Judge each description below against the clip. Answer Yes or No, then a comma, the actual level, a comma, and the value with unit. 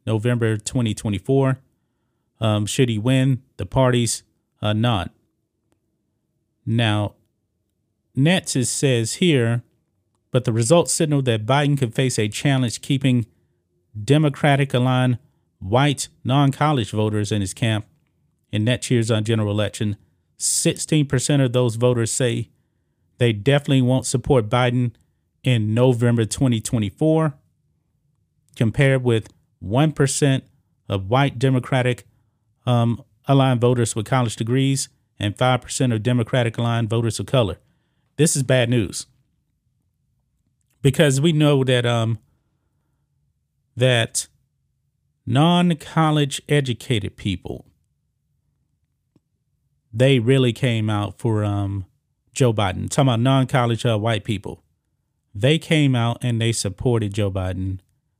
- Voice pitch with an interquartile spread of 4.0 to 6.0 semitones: No, average, 3.5 semitones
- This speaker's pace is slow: Yes, slow, 110 wpm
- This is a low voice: Yes, low, 120 Hz